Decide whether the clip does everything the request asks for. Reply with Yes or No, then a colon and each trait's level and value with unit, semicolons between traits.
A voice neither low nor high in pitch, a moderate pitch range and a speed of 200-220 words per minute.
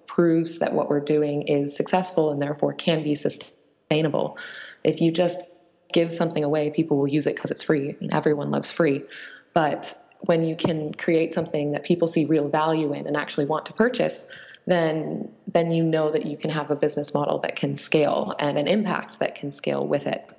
No: medium, 155 Hz; narrow, 2.2 semitones; fast, 205 wpm